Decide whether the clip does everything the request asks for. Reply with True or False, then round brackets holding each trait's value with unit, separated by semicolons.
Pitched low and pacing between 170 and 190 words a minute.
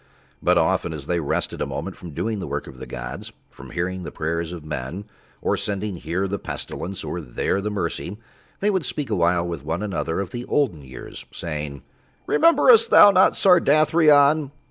True (95 Hz; 180 wpm)